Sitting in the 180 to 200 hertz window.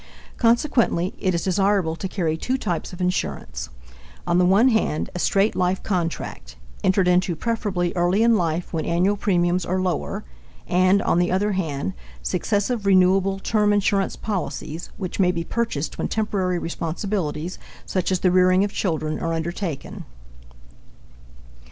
Yes: medium, 185 Hz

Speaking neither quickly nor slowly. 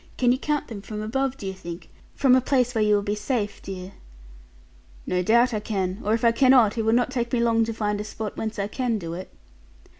No: fast, 245 wpm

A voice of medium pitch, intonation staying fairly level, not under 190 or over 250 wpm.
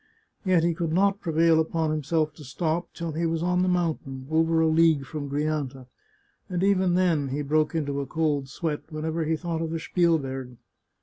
Yes: medium, 160 Hz; narrow, 2.2 semitones; average, 200 wpm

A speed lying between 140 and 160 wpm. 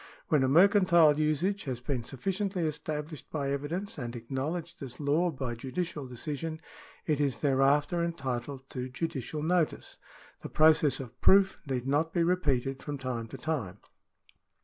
Yes: average, 150 wpm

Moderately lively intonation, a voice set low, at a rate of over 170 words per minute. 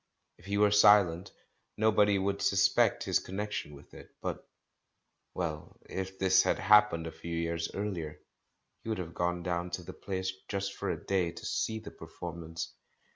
Yes: average, 3.1 semitones; very low, 95 Hz; average, 180 wpm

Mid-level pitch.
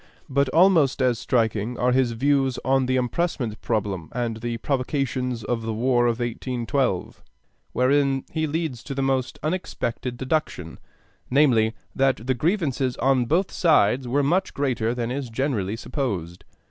No: low, 130 Hz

